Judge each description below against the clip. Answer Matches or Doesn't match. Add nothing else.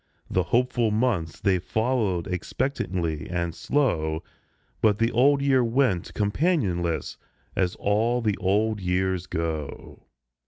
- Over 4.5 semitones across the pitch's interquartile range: Matches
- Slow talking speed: Matches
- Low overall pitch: Matches